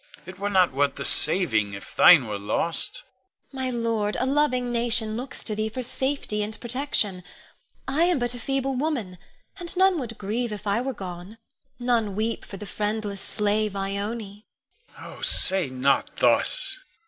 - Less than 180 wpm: Yes, average, 170 wpm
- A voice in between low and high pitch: No, high, 215 Hz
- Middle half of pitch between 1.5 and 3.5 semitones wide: No, average, 4.5 semitones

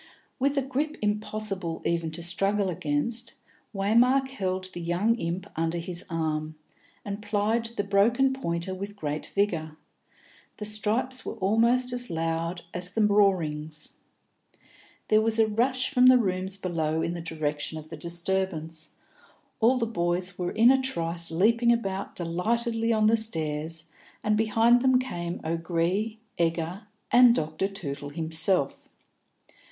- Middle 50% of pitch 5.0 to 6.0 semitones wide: Yes, average, 5.3 semitones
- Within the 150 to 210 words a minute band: No, average, 140 wpm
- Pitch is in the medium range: No, high, 195 Hz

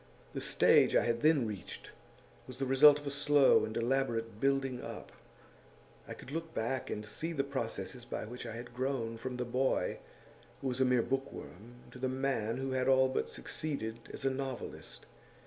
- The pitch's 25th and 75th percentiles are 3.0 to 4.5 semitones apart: No, narrow, 2.6 semitones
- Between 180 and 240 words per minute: Yes, average, 185 wpm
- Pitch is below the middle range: Yes, low, 130 Hz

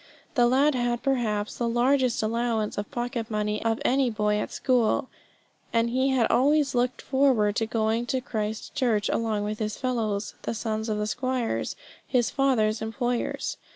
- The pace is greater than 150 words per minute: Yes, average, 165 wpm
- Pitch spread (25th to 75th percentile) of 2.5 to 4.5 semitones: Yes, average, 2.9 semitones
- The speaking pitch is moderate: No, high, 235 Hz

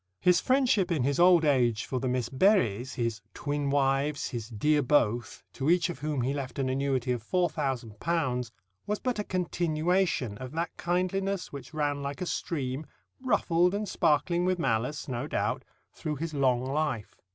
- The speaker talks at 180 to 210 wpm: No, average, 170 wpm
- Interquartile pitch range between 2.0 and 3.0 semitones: No, average, 5.3 semitones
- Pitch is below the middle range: No, medium, 145 Hz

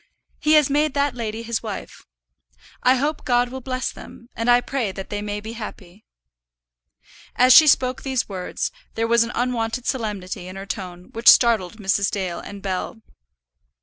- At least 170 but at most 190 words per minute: Yes, average, 175 wpm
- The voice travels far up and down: No, average, 4.0 semitones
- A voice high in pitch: Yes, high, 230 Hz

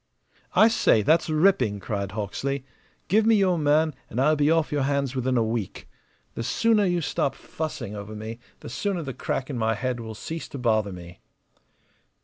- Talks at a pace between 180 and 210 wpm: Yes, average, 185 wpm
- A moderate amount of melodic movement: No, wide, 6.3 semitones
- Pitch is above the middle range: No, low, 135 Hz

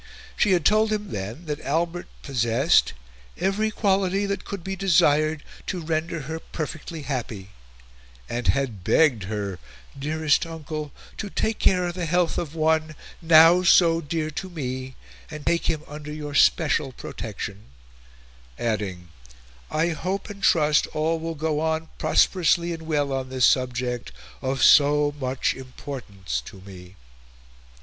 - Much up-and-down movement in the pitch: No, average, 4.5 semitones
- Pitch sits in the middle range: Yes, medium, 155 Hz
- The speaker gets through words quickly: No, average, 145 wpm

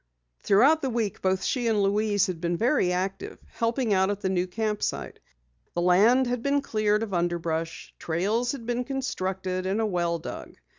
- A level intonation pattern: No, average, 4.3 semitones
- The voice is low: No, high, 205 Hz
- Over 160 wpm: Yes, average, 185 wpm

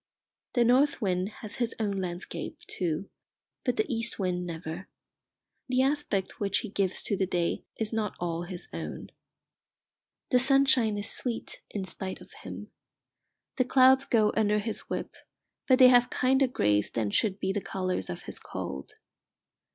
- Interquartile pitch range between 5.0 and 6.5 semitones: Yes, average, 5.3 semitones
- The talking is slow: No, average, 160 wpm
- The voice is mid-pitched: No, high, 205 Hz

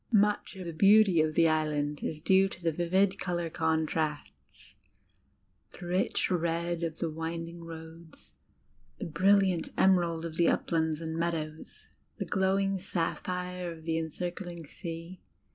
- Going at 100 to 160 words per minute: Yes, average, 140 wpm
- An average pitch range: No, narrow, 2.1 semitones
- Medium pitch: Yes, medium, 170 Hz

